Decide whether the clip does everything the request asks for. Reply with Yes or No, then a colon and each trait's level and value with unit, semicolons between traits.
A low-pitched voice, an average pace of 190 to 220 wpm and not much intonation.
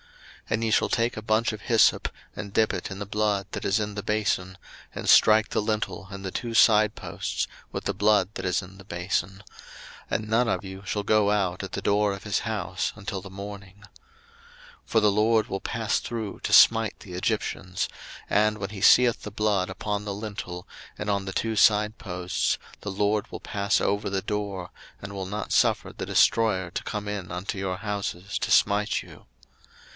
Yes: low, 105 Hz; average, 200 wpm; narrow, 1.8 semitones